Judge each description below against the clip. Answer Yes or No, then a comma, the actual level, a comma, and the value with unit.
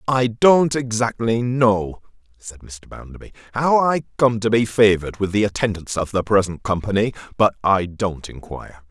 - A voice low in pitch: Yes, low, 110 Hz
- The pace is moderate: Yes, average, 160 wpm